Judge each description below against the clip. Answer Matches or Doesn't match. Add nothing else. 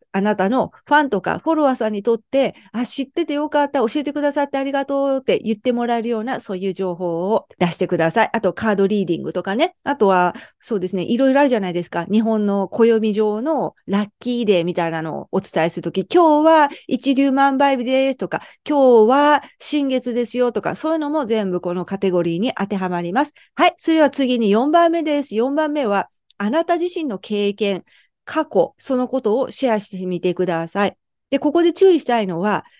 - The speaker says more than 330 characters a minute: Matches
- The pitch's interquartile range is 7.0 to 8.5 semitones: Doesn't match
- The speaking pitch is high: Matches